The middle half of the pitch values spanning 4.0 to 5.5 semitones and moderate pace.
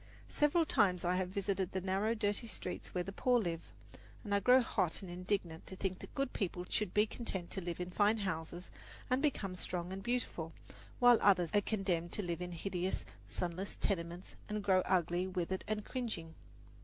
No: average, 3.1 semitones; average, 190 wpm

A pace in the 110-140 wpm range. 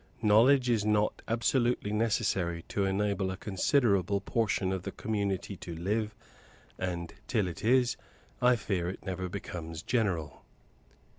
Yes: slow, 135 wpm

